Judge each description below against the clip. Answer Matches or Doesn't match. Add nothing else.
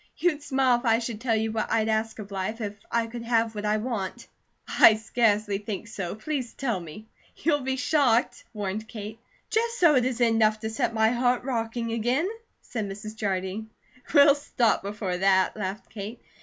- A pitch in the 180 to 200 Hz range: Doesn't match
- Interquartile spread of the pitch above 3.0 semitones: Doesn't match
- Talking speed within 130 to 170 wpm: Doesn't match